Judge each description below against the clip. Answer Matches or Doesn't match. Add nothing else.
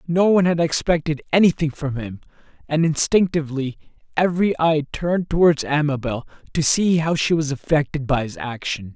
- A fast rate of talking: Doesn't match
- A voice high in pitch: Doesn't match